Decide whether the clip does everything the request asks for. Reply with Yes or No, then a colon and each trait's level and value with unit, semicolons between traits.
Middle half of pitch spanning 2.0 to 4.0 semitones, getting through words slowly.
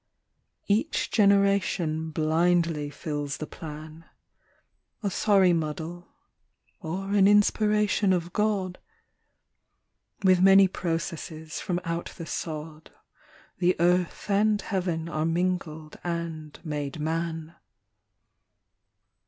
Yes: average, 3.4 semitones; slow, 95 wpm